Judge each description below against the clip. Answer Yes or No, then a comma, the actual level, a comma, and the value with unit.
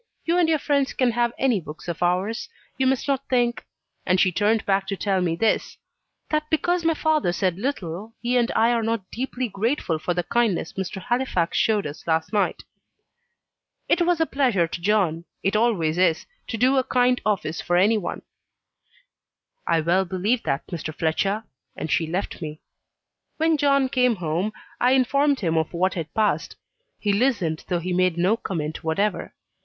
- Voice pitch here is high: Yes, high, 205 Hz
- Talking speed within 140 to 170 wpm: No, average, 180 wpm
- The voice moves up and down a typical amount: No, wide, 6.3 semitones